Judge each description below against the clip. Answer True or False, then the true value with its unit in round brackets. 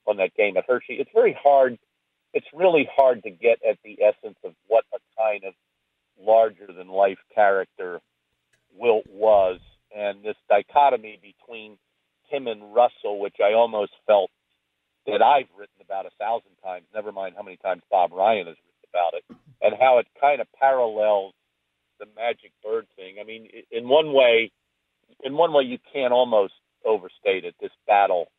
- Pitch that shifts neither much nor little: False (7.6 semitones)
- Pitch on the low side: True (110 Hz)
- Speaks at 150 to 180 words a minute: True (170 wpm)